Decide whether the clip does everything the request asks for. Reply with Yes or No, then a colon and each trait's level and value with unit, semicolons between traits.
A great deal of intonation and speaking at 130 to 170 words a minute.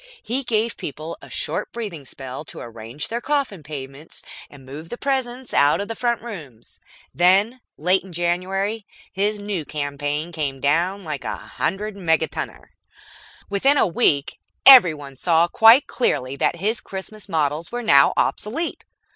Yes: wide, 6.8 semitones; average, 150 wpm